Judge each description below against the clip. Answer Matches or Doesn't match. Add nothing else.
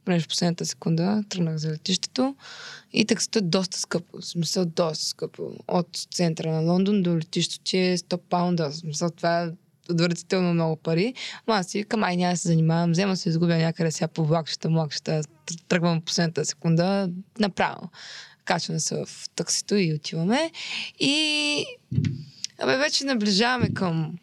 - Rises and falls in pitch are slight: Doesn't match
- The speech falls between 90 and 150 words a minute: Doesn't match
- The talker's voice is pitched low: Doesn't match